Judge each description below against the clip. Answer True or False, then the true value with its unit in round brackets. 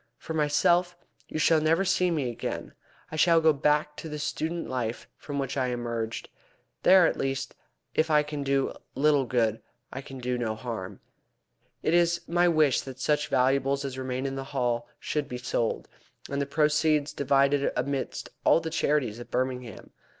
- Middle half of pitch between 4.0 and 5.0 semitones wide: False (3.4 semitones)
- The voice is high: False (140 Hz)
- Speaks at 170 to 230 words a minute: True (175 wpm)